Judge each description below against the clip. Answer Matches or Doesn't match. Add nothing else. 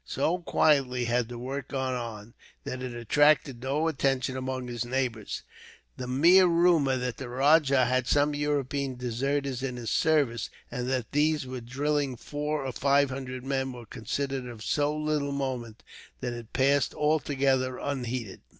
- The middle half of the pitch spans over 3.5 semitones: Doesn't match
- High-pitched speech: Doesn't match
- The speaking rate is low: Doesn't match